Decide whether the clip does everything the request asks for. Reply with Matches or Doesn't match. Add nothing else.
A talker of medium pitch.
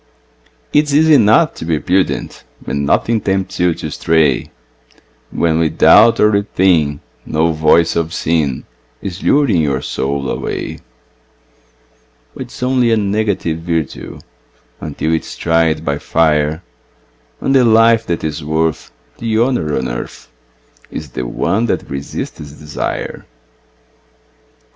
Doesn't match